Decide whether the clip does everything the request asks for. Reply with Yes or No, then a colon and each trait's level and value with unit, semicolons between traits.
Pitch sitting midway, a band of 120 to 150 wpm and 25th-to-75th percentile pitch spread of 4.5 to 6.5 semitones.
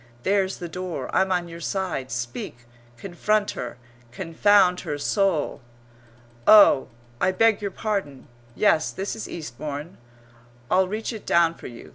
Yes: medium, 180 Hz; average, 140 wpm; average, 5.1 semitones